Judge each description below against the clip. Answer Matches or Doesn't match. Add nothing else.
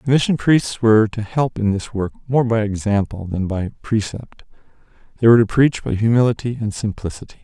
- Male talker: Matches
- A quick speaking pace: Doesn't match